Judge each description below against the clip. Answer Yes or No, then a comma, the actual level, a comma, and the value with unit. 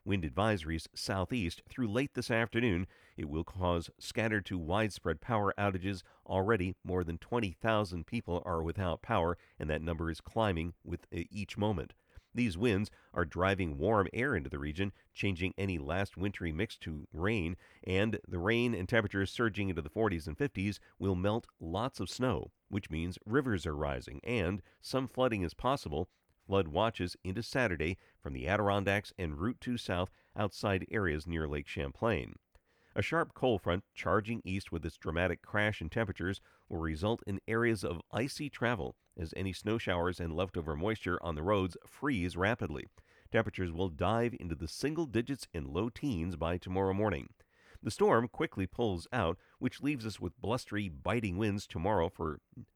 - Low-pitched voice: Yes, very low, 95 Hz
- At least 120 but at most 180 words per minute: Yes, average, 165 wpm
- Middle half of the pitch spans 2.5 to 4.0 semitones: No, average, 4.5 semitones